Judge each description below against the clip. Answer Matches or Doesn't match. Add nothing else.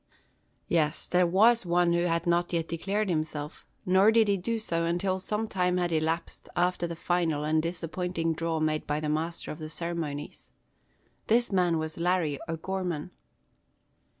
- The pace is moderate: Matches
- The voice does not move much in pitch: Matches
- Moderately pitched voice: Matches